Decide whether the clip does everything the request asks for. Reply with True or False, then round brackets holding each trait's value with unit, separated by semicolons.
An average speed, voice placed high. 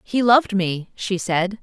True (185 wpm; 200 Hz)